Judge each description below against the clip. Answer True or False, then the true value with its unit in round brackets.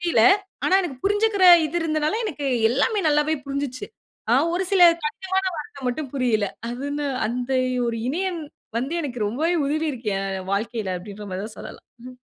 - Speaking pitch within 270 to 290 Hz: True (280 Hz)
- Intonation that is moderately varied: False (6.1 semitones)